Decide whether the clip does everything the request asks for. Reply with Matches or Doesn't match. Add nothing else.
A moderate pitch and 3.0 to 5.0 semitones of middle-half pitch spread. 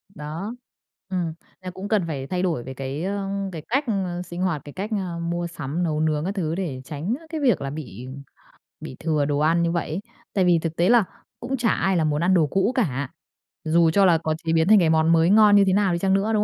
Matches